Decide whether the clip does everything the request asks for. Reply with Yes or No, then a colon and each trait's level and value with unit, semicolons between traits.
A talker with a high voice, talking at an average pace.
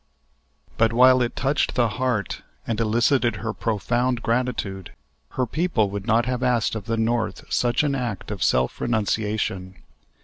No: low, 115 Hz; average, 150 wpm